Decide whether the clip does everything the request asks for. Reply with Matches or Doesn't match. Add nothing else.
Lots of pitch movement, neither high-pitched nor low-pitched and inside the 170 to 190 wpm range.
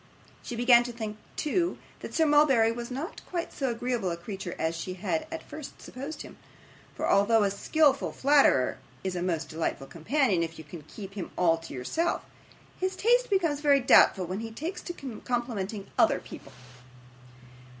Doesn't match